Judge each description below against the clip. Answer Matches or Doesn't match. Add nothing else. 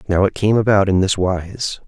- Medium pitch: Doesn't match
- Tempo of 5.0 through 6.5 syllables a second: Doesn't match